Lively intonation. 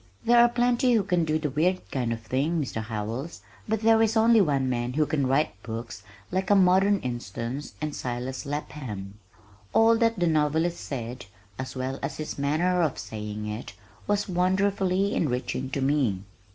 Yes: wide, 7.2 semitones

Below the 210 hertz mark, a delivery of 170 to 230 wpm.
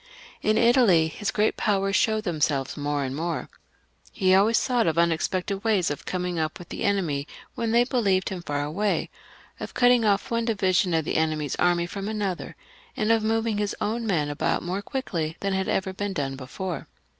Yes: high, 190 Hz; average, 190 wpm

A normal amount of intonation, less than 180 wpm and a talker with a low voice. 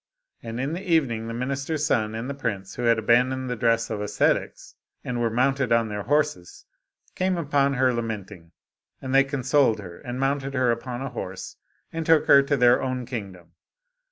No: average, 3.4 semitones; average, 190 wpm; low, 125 Hz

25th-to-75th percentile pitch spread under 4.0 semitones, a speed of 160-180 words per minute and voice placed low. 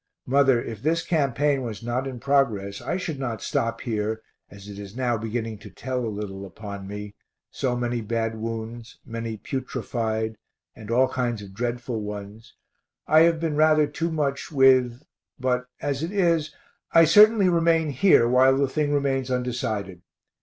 No: average, 4.3 semitones; average, 165 wpm; low, 125 Hz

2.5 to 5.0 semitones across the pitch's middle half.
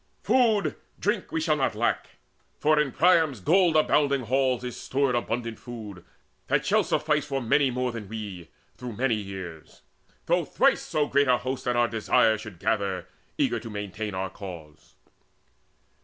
No: wide, 5.4 semitones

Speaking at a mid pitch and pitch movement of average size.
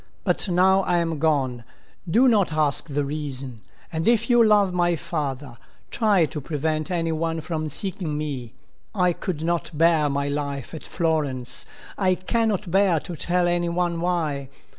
Yes: medium, 165 Hz; average, 3.5 semitones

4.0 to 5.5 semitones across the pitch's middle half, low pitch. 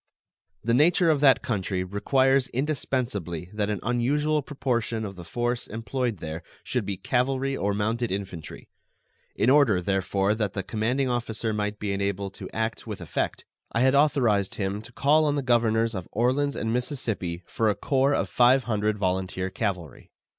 Yes: average, 4.8 semitones; low, 110 Hz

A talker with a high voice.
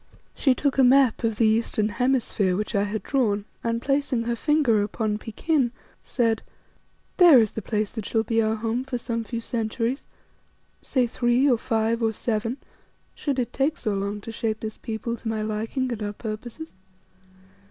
Yes: high, 230 Hz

